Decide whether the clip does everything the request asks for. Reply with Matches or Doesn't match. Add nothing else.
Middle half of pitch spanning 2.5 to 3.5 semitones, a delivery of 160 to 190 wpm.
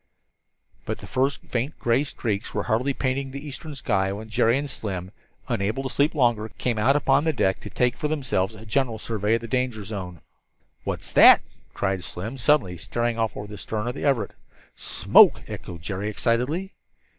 Doesn't match